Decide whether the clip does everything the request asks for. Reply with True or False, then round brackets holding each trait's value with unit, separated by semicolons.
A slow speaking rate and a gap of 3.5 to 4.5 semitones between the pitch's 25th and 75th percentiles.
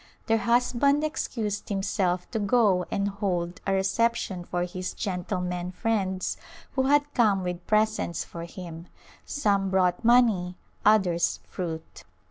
True (125 wpm; 4.0 semitones)